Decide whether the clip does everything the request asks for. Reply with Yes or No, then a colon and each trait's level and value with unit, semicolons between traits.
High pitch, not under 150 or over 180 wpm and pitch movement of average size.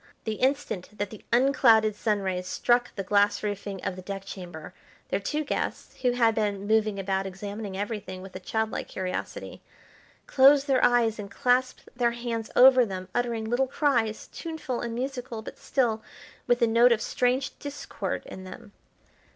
Yes: high, 220 Hz; average, 165 wpm; average, 3.7 semitones